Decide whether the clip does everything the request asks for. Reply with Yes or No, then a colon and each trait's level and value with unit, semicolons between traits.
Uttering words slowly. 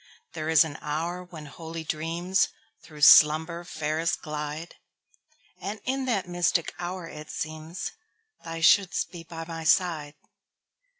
Yes: slow, 115 wpm